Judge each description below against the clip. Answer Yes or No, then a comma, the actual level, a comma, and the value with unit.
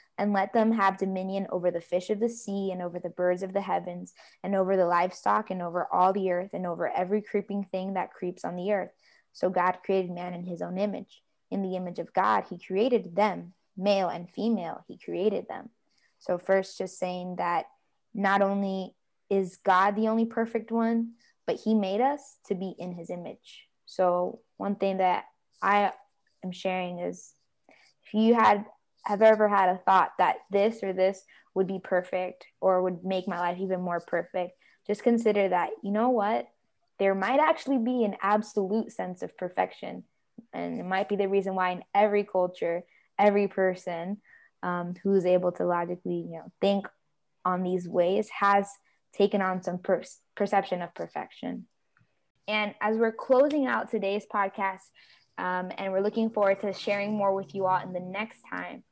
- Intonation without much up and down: Yes, narrow, 2.3 semitones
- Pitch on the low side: No, high, 195 Hz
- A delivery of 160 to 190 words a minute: Yes, average, 185 wpm